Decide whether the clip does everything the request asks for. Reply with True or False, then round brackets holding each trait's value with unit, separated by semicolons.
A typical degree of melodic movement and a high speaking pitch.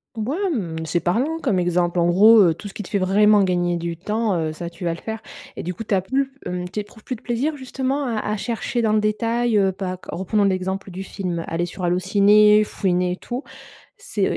True (3.8 semitones; 200 Hz)